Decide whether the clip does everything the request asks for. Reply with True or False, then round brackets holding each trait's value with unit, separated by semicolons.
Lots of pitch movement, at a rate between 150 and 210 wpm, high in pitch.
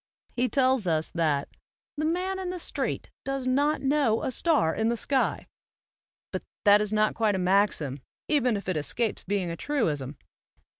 True (7.3 semitones; 180 wpm; 225 Hz)